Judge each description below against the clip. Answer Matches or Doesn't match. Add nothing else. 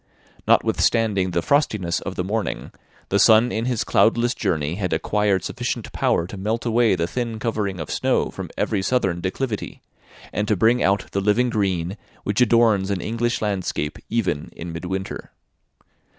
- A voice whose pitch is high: Doesn't match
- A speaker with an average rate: Matches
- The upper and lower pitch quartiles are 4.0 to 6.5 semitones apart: Doesn't match